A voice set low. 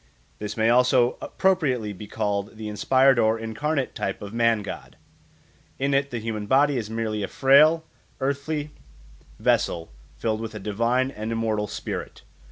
Yes: low, 115 Hz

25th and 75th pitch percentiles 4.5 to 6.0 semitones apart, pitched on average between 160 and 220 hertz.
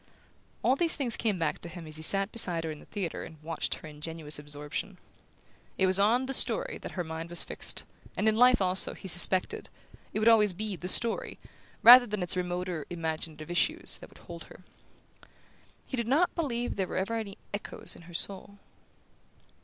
Yes: average, 5.2 semitones; medium, 185 Hz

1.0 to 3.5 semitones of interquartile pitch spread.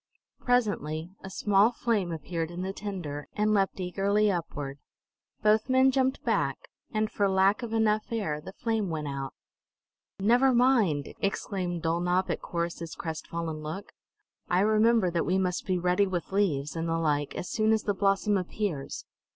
No: average, 4.2 semitones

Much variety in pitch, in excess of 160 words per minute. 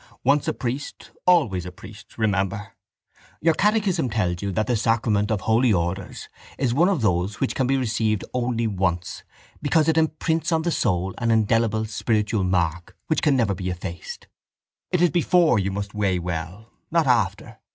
Yes: wide, 6.1 semitones; average, 170 wpm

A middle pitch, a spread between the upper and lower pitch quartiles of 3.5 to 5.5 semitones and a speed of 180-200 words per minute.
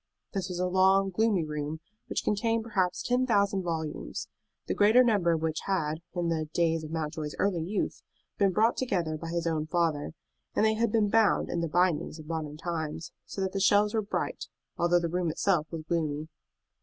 Yes: medium, 175 Hz; average, 4.0 semitones; average, 195 wpm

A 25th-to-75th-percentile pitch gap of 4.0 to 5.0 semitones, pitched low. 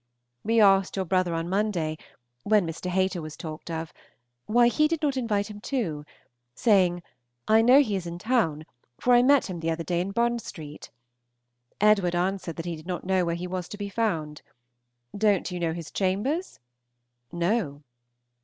No: average, 4.3 semitones; medium, 185 Hz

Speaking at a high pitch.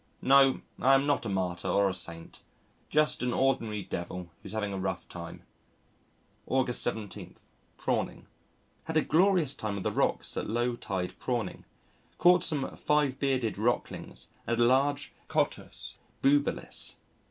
No: low, 125 Hz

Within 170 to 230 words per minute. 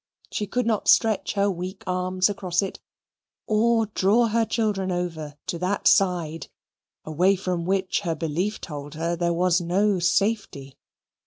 No: average, 150 wpm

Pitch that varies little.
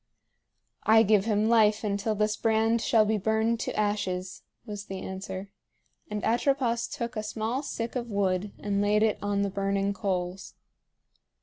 Yes: narrow, 1.9 semitones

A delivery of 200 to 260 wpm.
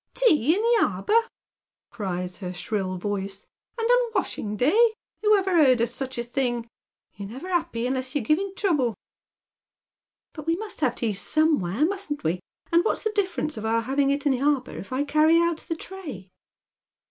Yes: fast, 205 wpm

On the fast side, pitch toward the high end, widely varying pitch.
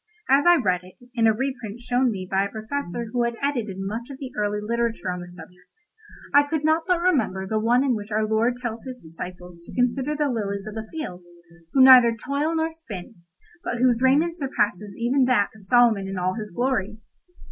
No: fast, 210 wpm; high, 235 Hz; average, 4.8 semitones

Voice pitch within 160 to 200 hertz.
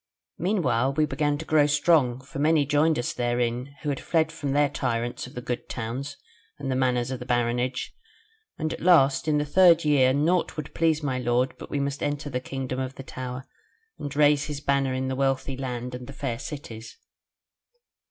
No: low, 135 Hz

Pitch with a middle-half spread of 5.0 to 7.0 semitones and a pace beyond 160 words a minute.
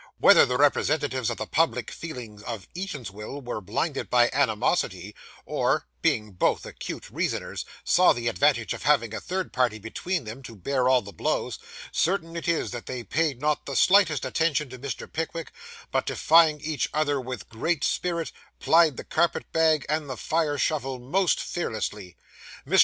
Yes: wide, 5.5 semitones; average, 170 wpm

